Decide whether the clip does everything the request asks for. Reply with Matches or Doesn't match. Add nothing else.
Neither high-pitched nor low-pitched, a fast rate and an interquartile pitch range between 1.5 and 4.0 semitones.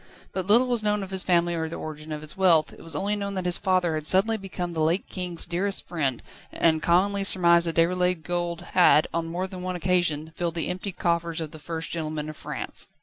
Matches